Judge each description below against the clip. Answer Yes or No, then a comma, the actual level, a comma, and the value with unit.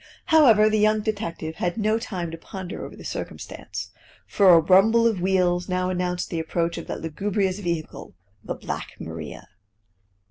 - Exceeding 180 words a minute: No, average, 165 wpm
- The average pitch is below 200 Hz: Yes, medium, 185 Hz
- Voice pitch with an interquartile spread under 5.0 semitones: Yes, average, 3.7 semitones